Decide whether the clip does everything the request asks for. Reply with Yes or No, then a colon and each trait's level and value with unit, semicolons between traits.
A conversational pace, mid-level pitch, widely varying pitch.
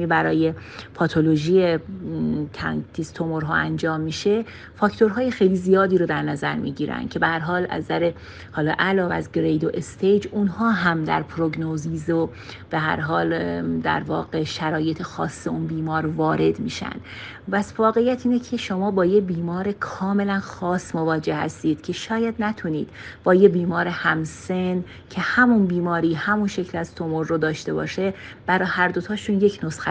No: average, 145 wpm; medium, 170 Hz; average, 3.7 semitones